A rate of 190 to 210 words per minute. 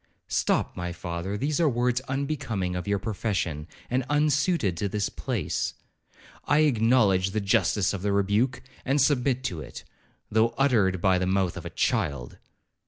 No: average, 155 wpm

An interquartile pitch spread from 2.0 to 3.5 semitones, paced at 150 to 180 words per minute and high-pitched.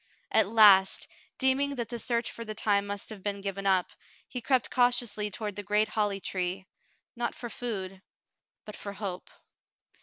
Yes: average, 3.0 semitones; average, 170 wpm; high, 210 Hz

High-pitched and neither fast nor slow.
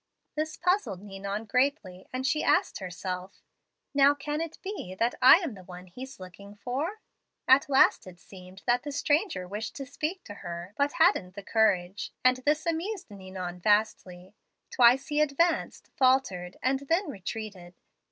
Yes: high, 240 Hz; average, 160 wpm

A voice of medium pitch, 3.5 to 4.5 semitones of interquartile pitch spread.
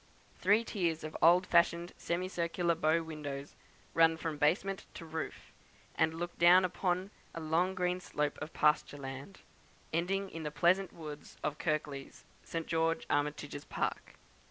No: medium, 165 Hz; average, 2.8 semitones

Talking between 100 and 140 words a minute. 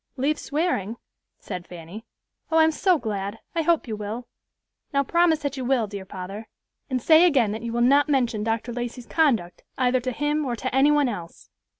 No: average, 195 wpm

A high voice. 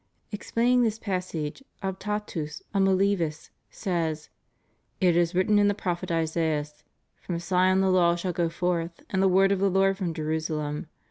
No: medium, 180 Hz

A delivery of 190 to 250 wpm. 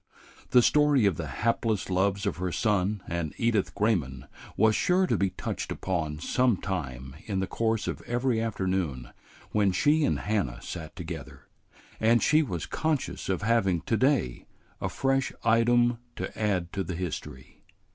No: average, 160 wpm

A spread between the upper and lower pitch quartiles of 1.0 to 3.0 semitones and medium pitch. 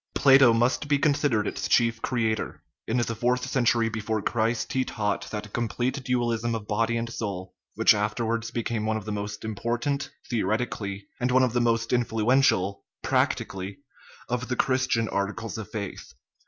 No: narrow, 2.5 semitones; low, 115 Hz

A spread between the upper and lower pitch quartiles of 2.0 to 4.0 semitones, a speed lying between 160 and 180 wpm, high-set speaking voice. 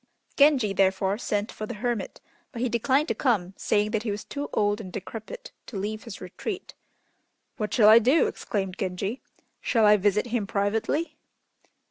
Yes: average, 3.1 semitones; average, 170 wpm; high, 215 Hz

